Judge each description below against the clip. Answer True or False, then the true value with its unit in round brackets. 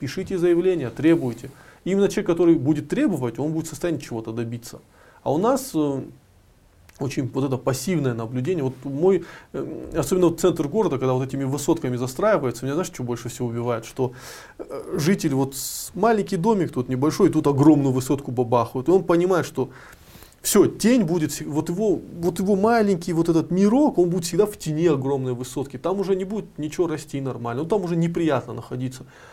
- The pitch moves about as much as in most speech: False (5.7 semitones)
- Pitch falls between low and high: True (155 Hz)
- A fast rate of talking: True (175 wpm)